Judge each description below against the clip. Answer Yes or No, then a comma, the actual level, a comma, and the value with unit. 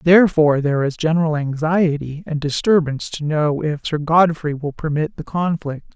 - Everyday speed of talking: Yes, average, 160 wpm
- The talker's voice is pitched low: No, medium, 155 Hz